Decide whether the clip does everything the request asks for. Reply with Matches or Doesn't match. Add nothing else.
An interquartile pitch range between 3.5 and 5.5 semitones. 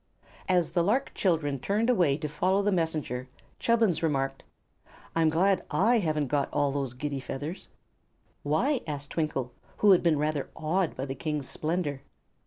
Matches